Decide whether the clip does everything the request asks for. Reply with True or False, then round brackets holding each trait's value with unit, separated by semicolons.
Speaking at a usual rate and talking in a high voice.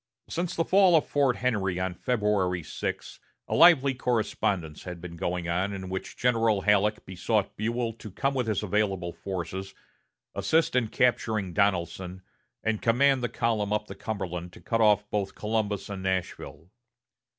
False (160 wpm; 105 Hz)